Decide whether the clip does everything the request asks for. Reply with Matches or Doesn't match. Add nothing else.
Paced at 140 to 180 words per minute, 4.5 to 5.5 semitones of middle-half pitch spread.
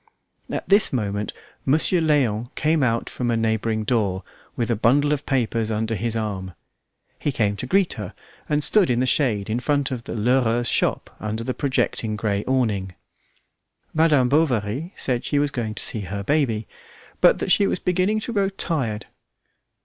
Matches